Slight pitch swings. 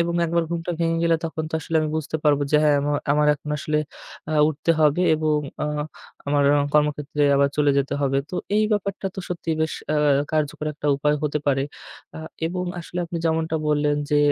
Yes: narrow, 2.1 semitones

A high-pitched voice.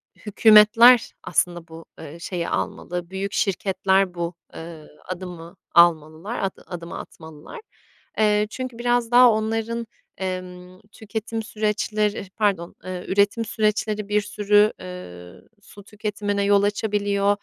Yes: high, 200 Hz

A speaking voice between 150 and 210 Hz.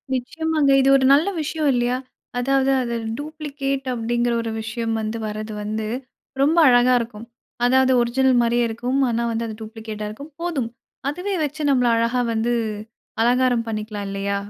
No: high, 245 Hz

